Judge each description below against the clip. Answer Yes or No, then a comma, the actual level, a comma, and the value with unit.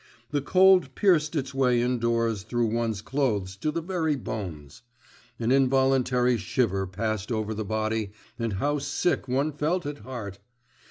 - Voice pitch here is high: No, low, 125 Hz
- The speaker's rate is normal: Yes, average, 150 wpm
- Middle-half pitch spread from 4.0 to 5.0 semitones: Yes, average, 4.7 semitones